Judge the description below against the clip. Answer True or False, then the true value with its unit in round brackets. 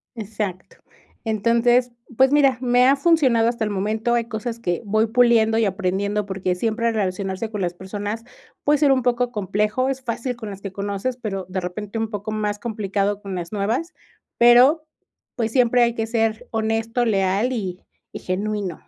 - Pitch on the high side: True (220 Hz)